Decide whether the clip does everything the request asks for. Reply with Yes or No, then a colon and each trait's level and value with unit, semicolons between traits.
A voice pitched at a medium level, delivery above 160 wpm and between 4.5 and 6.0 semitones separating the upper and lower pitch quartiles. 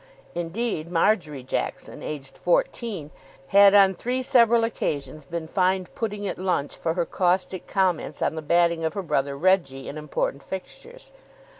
No: medium, 180 Hz; average, 150 wpm; average, 4.8 semitones